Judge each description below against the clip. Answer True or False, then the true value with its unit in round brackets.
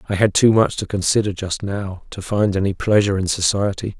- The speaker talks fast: True (210 wpm)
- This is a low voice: True (100 Hz)